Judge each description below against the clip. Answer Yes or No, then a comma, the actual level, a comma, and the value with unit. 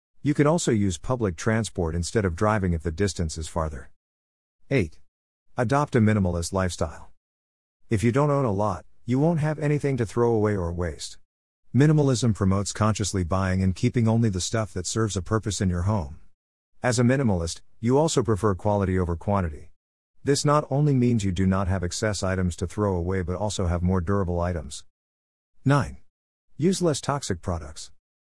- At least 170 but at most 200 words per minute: Yes, average, 175 wpm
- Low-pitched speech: Yes, very low, 95 Hz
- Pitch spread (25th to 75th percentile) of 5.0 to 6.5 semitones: Yes, wide, 5.4 semitones